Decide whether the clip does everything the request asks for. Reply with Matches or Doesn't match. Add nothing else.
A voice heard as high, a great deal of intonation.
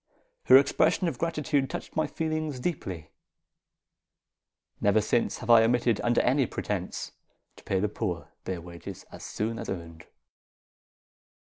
Doesn't match